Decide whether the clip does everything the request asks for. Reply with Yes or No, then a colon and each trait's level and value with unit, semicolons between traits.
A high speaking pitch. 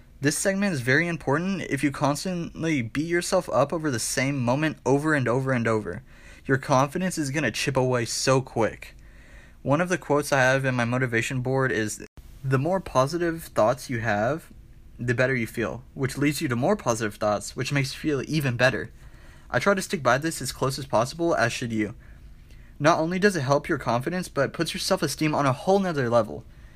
No: low, 135 Hz